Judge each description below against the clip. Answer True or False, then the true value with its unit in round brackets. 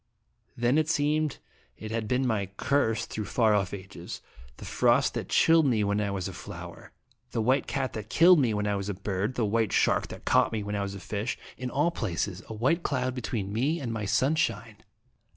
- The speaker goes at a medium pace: False (215 wpm)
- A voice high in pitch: False (110 Hz)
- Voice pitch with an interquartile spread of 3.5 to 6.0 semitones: True (4.2 semitones)